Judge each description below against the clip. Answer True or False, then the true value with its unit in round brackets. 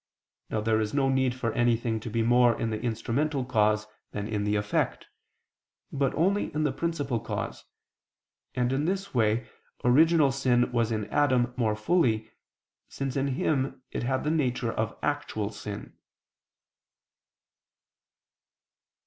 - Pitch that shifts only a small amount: False (3.8 semitones)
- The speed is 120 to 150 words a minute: True (140 wpm)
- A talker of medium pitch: False (125 Hz)